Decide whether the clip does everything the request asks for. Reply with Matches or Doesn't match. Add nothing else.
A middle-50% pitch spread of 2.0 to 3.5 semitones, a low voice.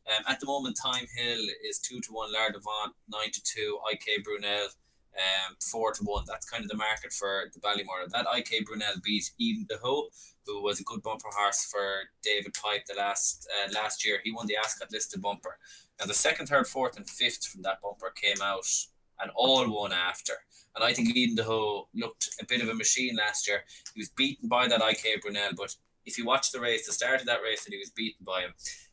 Doesn't match